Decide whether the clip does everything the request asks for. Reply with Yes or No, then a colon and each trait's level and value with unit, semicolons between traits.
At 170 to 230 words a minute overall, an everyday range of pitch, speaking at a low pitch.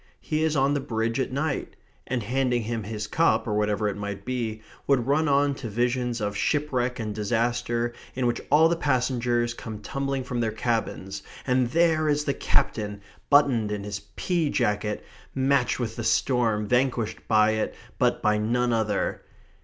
Yes: average, 175 wpm; average, 3.9 semitones; low, 120 Hz